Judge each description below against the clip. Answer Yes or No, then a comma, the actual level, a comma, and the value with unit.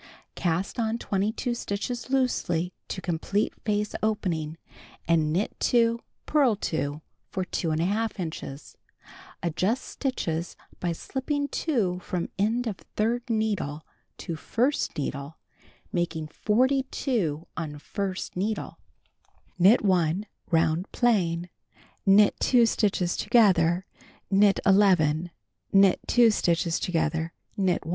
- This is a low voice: No, high, 190 Hz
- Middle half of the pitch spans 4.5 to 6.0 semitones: Yes, average, 5.2 semitones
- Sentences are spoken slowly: Yes, slow, 110 wpm